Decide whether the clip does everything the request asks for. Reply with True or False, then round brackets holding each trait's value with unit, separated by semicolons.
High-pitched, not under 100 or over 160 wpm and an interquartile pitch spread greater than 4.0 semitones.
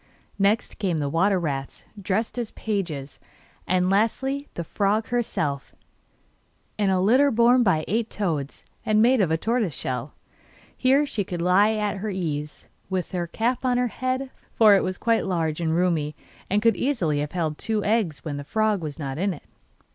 False (195 Hz; 175 wpm; 5.6 semitones)